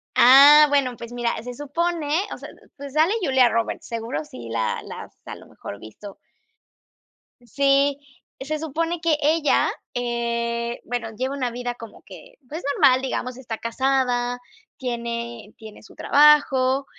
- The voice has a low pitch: No, very high, 255 Hz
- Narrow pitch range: No, average, 3.4 semitones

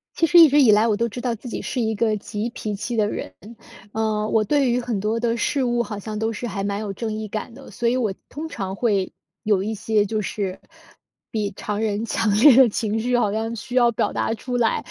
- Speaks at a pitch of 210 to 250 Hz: Yes, high, 220 Hz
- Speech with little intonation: Yes, narrow, 2.3 semitones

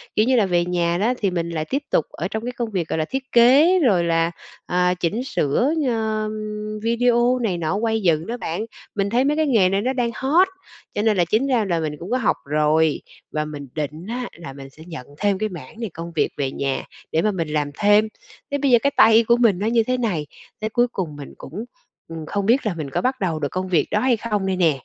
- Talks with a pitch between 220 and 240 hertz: No, high, 205 Hz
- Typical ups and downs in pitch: No, wide, 6.1 semitones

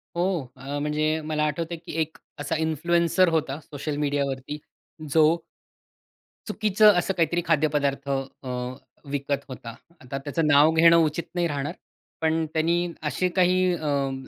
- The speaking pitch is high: No, medium, 155 Hz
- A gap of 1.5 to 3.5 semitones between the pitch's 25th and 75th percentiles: Yes, average, 3.0 semitones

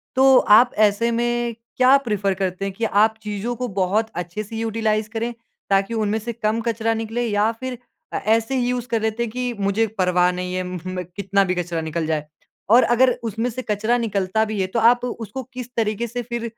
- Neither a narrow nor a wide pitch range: Yes, average, 3.1 semitones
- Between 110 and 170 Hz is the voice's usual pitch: No, high, 220 Hz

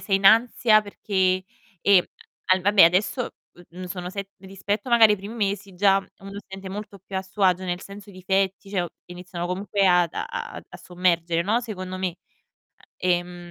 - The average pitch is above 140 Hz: Yes, high, 190 Hz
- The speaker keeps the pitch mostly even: Yes, narrow, 2.0 semitones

